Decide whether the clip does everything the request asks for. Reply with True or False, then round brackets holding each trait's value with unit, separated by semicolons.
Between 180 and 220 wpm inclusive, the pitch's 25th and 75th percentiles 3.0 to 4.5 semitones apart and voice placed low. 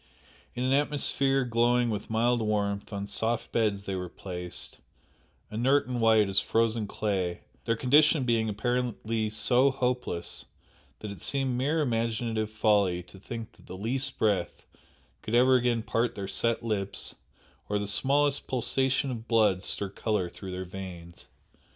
False (150 wpm; 3.6 semitones; 115 Hz)